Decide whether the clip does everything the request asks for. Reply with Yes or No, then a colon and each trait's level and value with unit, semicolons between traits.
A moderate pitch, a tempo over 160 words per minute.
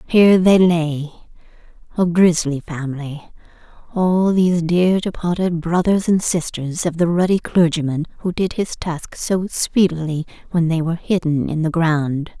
No: medium, 170 Hz; average, 145 wpm